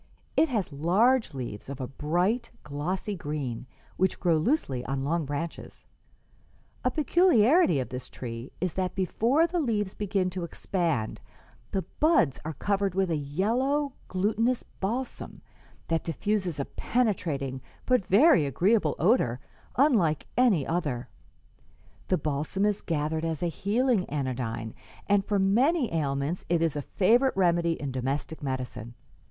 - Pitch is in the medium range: Yes, medium, 175 Hz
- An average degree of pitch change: No, wide, 6.9 semitones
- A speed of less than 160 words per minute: Yes, average, 140 wpm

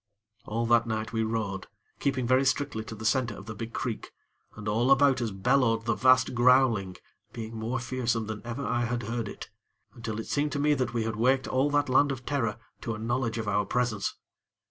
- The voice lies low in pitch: Yes, low, 115 Hz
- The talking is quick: Yes, fast, 210 wpm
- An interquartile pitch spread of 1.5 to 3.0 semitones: Yes, average, 2.7 semitones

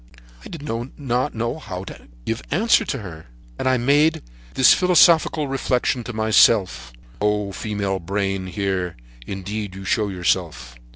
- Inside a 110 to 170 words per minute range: Yes, slow, 135 wpm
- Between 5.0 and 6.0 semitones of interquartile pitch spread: Yes, wide, 5.5 semitones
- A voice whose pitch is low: Yes, low, 105 Hz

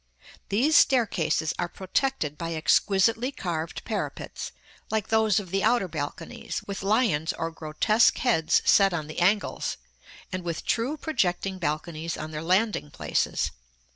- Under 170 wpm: Yes, average, 140 wpm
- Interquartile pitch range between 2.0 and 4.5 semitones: No, average, 5.3 semitones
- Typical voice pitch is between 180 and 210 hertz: Yes, medium, 185 Hz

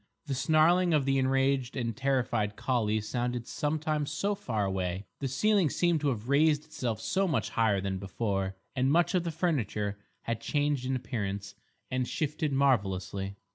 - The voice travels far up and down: Yes, wide, 6.2 semitones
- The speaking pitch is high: No, low, 130 Hz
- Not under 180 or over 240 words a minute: No, average, 165 wpm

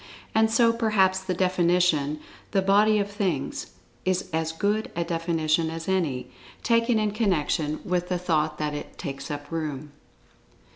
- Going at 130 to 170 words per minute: Yes, average, 150 wpm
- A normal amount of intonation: Yes, average, 4.6 semitones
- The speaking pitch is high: No, medium, 180 Hz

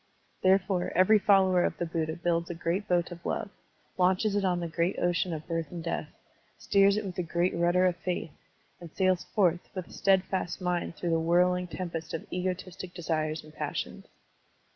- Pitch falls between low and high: Yes, medium, 175 Hz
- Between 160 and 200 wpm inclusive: Yes, average, 190 wpm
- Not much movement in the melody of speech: Yes, narrow, 1.7 semitones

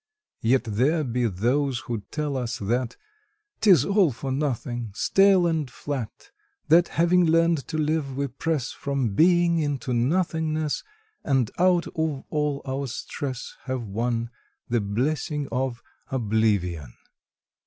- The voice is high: No, low, 135 Hz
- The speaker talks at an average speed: No, slow, 130 wpm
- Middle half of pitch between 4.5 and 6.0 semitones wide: Yes, average, 4.8 semitones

